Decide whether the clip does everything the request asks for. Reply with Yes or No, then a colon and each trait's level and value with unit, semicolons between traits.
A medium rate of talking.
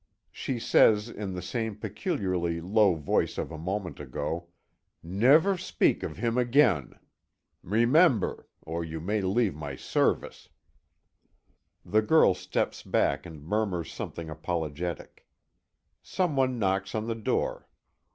No: slow, 120 wpm